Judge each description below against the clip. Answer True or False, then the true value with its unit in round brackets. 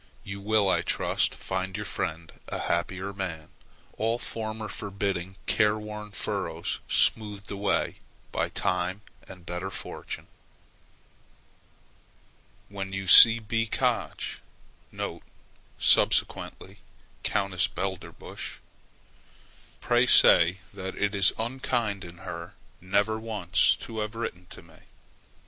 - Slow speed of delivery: True (105 wpm)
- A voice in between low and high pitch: False (100 Hz)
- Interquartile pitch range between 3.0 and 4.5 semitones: False (2.5 semitones)